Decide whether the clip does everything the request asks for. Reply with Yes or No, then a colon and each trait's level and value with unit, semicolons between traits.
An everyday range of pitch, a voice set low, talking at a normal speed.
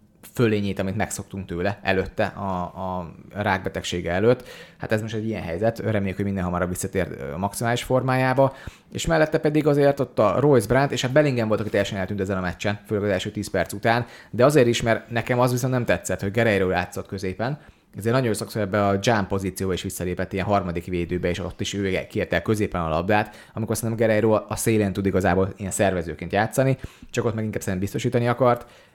No: average, 3.5 semitones; low, 105 Hz; fast, 200 wpm